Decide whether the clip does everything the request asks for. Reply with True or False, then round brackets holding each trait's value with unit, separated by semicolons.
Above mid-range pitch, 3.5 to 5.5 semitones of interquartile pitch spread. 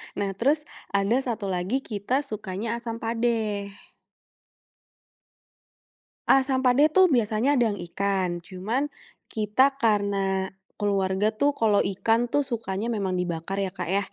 True (215 Hz; 3.9 semitones)